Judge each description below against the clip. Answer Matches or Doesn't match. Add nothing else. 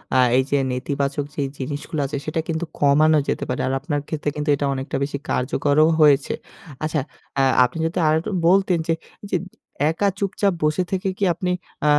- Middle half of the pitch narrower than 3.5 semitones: Matches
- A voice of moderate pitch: Matches